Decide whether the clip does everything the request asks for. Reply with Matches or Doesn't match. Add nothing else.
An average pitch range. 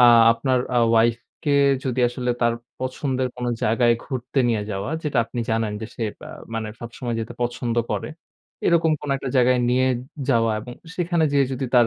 Doesn't match